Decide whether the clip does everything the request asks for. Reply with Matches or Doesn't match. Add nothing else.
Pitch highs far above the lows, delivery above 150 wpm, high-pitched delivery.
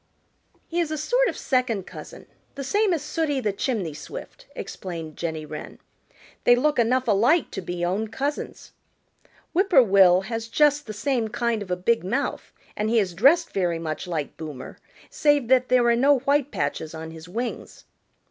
Matches